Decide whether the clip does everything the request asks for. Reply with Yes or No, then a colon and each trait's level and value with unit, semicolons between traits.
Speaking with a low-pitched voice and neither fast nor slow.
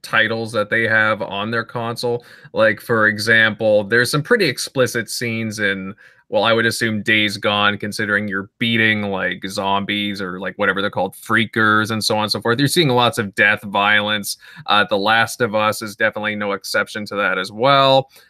Yes: low, 110 Hz; average, 190 wpm